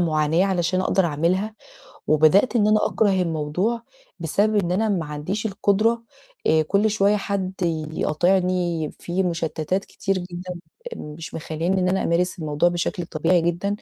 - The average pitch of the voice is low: No, medium, 180 Hz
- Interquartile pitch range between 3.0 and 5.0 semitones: Yes, average, 3.4 semitones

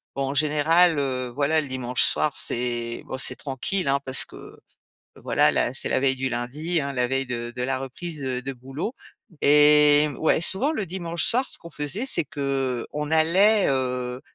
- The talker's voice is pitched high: No, medium, 140 Hz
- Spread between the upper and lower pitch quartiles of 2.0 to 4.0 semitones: Yes, average, 3.6 semitones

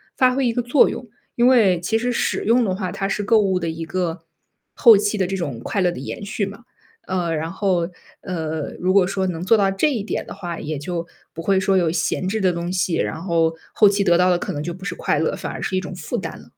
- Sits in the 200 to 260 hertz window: No, medium, 185 Hz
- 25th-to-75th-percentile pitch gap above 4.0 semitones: No, average, 3.2 semitones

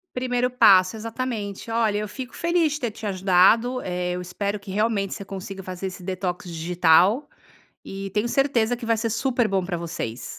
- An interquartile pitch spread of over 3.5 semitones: Yes, average, 4.3 semitones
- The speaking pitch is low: No, high, 205 Hz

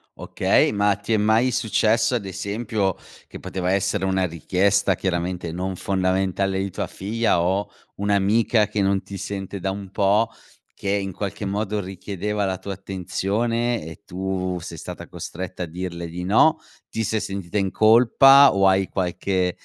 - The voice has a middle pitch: No, very low, 95 Hz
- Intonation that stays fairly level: Yes, narrow, 2.1 semitones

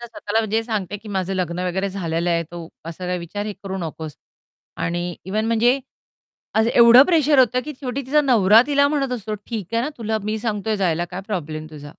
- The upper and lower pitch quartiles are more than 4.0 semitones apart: Yes, average, 4.9 semitones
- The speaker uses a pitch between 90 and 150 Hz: No, high, 205 Hz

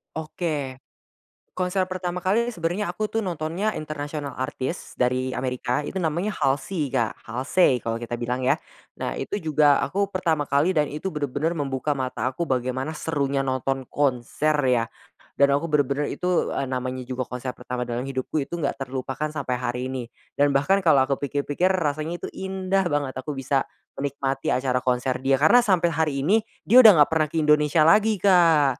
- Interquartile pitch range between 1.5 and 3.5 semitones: No, average, 4.5 semitones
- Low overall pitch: No, medium, 145 Hz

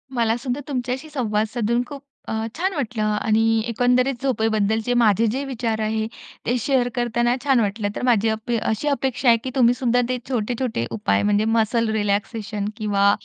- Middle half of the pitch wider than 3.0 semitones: No, narrow, 2.5 semitones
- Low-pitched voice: No, high, 230 Hz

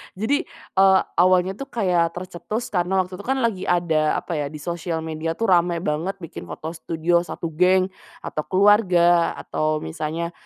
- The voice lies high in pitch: No, medium, 175 Hz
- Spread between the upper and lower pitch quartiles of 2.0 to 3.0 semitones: Yes, narrow, 2.6 semitones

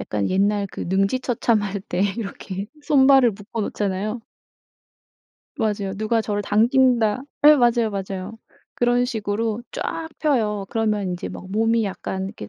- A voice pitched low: No, high, 215 Hz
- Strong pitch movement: No, average, 3.2 semitones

